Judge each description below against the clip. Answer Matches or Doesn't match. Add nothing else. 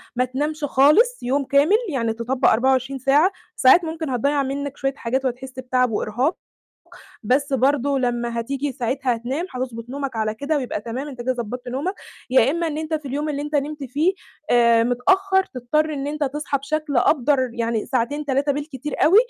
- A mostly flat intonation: Doesn't match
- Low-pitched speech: Doesn't match